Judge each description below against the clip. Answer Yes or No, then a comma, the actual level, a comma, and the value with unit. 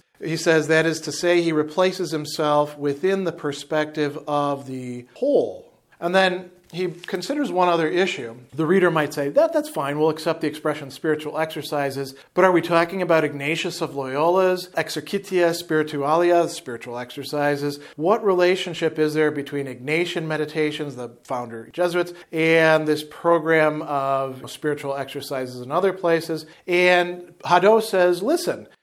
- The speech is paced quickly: No, average, 145 wpm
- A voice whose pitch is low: No, medium, 160 Hz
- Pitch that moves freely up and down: No, average, 3.4 semitones